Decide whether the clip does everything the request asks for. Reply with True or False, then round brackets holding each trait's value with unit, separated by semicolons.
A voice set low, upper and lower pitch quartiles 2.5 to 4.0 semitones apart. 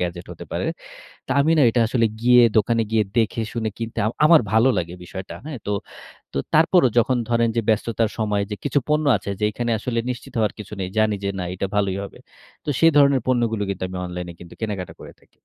True (110 Hz; 3.6 semitones)